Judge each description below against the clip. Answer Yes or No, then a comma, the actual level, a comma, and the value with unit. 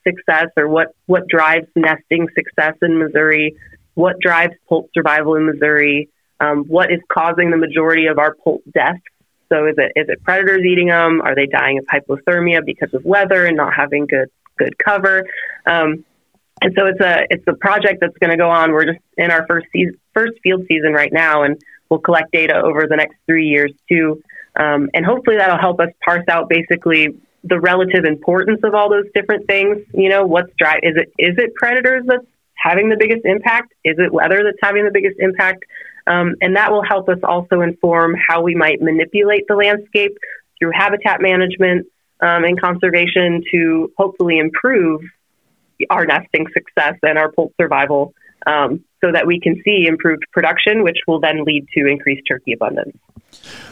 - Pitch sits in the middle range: Yes, medium, 170 Hz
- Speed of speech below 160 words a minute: No, average, 185 wpm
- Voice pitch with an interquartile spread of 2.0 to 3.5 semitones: Yes, average, 3.1 semitones